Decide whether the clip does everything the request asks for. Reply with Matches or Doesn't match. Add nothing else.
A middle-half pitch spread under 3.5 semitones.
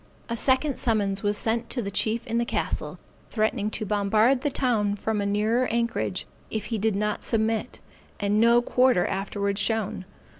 Matches